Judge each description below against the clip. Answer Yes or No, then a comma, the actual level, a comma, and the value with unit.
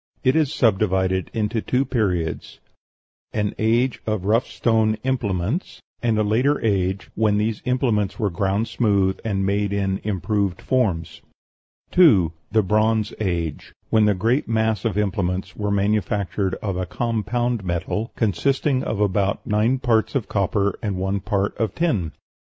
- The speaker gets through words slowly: No, average, 145 wpm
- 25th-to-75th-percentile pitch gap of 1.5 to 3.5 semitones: Yes, average, 2.9 semitones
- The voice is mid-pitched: No, low, 105 Hz